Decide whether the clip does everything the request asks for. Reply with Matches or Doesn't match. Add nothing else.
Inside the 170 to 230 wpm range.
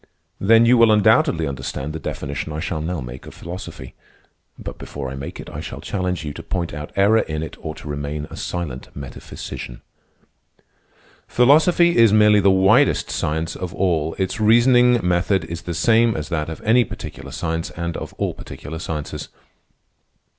Matches